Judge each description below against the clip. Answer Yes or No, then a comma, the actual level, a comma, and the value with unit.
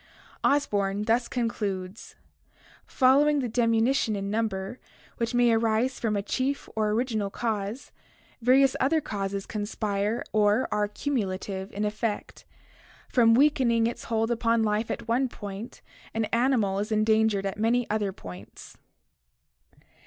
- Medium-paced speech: No, slow, 130 wpm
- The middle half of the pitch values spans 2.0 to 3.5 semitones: Yes, average, 2.8 semitones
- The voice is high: Yes, high, 225 Hz